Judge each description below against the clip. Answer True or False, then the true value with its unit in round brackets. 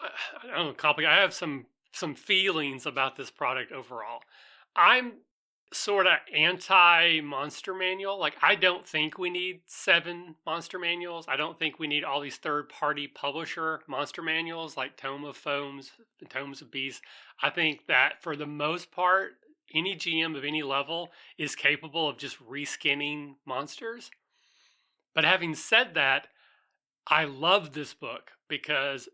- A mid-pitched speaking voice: True (160 Hz)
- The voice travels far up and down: False (3.6 semitones)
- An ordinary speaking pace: True (155 wpm)